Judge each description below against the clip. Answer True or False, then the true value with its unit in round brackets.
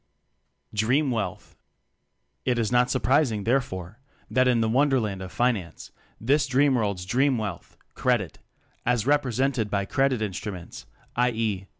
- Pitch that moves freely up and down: False (4.2 semitones)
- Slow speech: True (130 wpm)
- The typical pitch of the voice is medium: False (120 Hz)